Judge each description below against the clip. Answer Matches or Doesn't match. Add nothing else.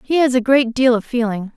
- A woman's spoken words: Matches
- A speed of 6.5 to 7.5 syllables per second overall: Doesn't match